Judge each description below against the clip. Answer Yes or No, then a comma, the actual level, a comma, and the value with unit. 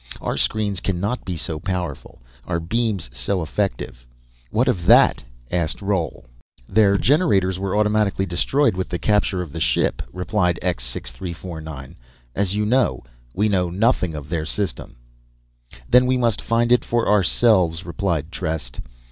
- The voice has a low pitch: Yes, very low, 95 Hz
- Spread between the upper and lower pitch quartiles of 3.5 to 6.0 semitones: Yes, average, 4.0 semitones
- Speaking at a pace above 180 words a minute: No, average, 150 wpm